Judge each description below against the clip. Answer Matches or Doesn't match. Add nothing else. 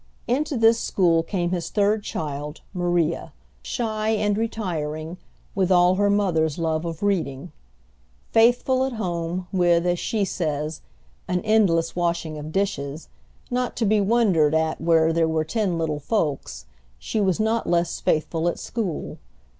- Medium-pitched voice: Matches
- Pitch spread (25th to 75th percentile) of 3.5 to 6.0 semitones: Matches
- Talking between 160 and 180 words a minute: Doesn't match